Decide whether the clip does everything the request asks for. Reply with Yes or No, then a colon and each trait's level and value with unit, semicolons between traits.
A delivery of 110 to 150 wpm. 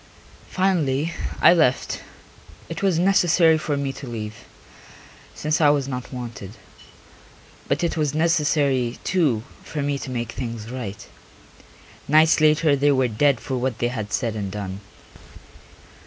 Yes: average, 140 wpm